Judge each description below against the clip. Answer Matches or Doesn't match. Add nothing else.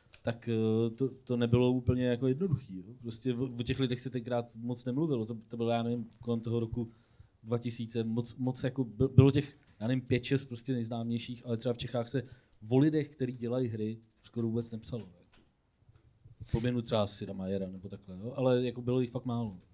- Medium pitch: Doesn't match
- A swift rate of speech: Matches